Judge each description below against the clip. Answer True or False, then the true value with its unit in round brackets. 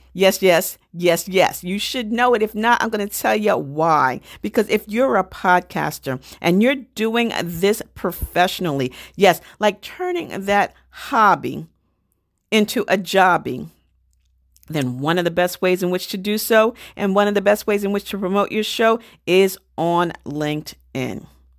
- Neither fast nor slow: True (165 wpm)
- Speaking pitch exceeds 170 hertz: True (190 Hz)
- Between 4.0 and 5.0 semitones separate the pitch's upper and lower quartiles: True (4.6 semitones)